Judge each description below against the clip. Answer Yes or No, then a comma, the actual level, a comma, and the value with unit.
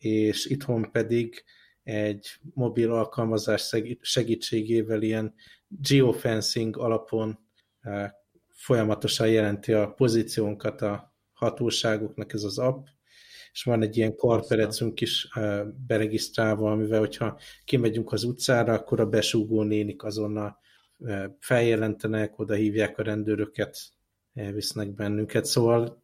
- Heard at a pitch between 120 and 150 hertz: No, low, 110 Hz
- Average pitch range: No, narrow, 1.6 semitones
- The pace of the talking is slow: Yes, slow, 100 wpm